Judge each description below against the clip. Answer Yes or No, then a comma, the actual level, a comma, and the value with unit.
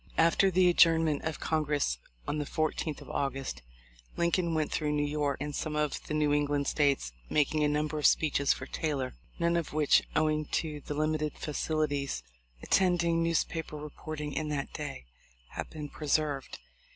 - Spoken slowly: No, average, 165 wpm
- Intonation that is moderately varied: No, narrow, 1.5 semitones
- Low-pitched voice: No, medium, 150 Hz